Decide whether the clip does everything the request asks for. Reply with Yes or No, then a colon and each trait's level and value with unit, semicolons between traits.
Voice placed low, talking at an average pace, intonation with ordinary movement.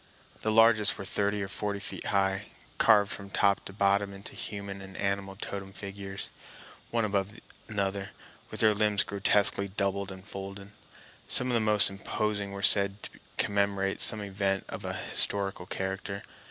No: low, 100 Hz; average, 160 wpm; narrow, 1.0 semitones